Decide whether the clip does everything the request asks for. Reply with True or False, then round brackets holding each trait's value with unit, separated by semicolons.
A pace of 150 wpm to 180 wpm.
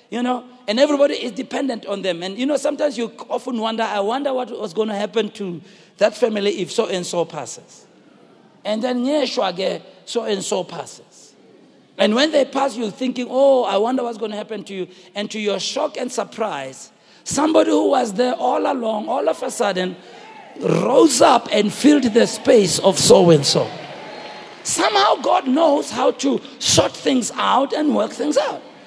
True (175 wpm)